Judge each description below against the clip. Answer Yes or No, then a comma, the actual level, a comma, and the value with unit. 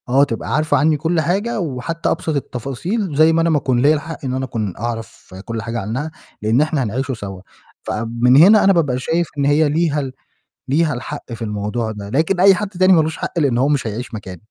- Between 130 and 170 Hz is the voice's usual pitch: Yes, medium, 140 Hz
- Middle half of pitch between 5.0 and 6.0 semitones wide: Yes, wide, 5.5 semitones